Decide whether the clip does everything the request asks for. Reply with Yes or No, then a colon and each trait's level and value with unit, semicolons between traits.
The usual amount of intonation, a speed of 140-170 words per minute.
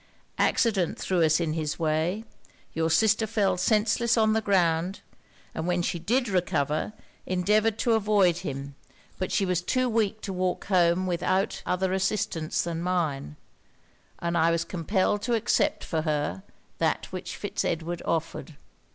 Yes: average, 4.1 semitones; average, 150 wpm